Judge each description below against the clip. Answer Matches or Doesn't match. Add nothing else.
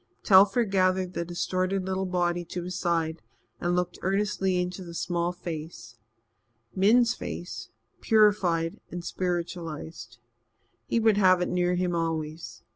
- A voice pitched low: Doesn't match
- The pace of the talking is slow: Matches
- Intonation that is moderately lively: Doesn't match